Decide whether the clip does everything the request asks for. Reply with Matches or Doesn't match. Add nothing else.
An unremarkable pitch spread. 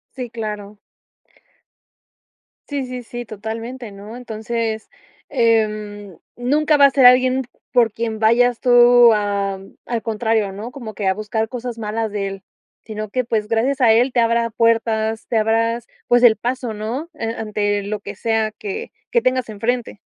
Doesn't match